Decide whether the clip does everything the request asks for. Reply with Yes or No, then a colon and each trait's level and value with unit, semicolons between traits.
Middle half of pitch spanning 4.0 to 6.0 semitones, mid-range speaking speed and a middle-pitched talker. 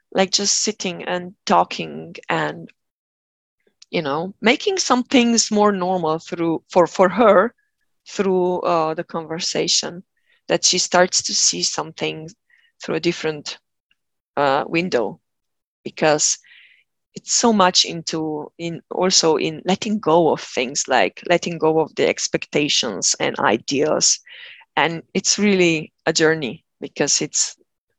No: average, 5.0 semitones; slow, 125 wpm; medium, 180 Hz